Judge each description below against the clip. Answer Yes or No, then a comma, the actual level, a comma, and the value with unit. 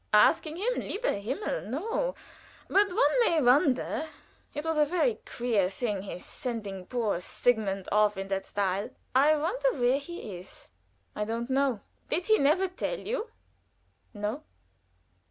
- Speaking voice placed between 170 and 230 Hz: No, very high, 260 Hz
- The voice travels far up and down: Yes, wide, 8.9 semitones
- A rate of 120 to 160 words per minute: Yes, average, 145 wpm